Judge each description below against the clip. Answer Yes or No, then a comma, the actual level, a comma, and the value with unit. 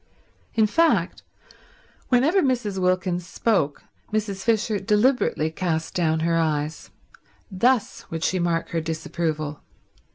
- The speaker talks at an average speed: No, slow, 110 wpm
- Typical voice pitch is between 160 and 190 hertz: Yes, medium, 185 Hz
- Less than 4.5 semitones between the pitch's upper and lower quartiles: No, average, 5.3 semitones